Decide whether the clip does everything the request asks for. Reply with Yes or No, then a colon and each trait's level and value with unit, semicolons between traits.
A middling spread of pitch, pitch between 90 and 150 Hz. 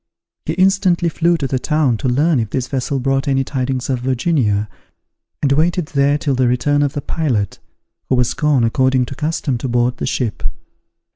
Yes: average, 3.3 semitones; low, 135 Hz